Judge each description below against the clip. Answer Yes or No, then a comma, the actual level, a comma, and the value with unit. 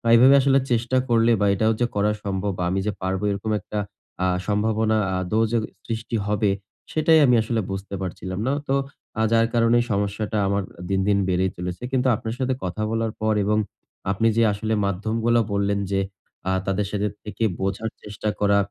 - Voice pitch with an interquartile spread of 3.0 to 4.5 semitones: No, narrow, 2.5 semitones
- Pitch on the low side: Yes, low, 105 Hz